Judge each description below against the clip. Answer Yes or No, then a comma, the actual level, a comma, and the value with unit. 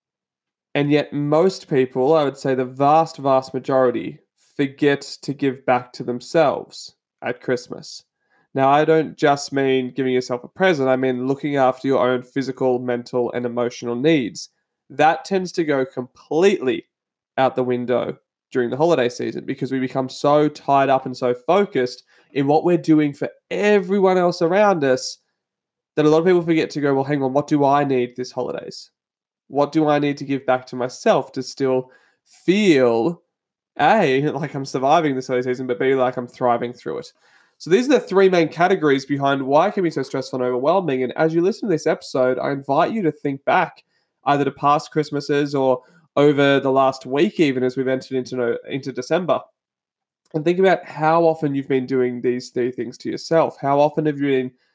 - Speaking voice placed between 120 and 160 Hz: Yes, medium, 140 Hz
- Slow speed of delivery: No, average, 190 wpm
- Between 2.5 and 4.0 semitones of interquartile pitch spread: Yes, average, 3.5 semitones